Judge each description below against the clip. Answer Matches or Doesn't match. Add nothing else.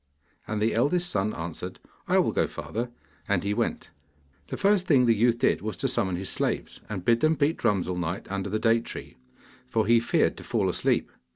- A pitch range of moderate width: Matches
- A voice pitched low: Matches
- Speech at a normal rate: Doesn't match